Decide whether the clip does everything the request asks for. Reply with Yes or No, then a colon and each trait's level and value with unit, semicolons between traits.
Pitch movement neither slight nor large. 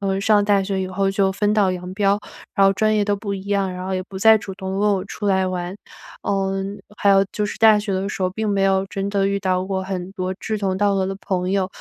No: narrow, 1.2 semitones